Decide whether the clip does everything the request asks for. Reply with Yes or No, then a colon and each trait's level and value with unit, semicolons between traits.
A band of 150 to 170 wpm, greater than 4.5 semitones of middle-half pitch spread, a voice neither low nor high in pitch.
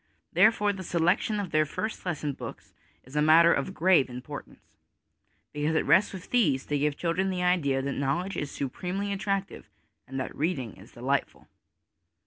Yes: average, 165 wpm; average, 5.2 semitones; medium, 165 Hz